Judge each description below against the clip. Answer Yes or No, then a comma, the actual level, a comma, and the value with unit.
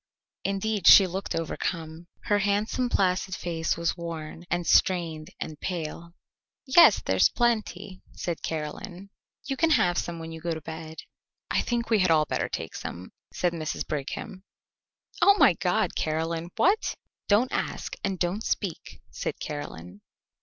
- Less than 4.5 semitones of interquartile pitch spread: Yes, average, 3.9 semitones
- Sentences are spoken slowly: No, average, 155 wpm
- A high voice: No, medium, 175 Hz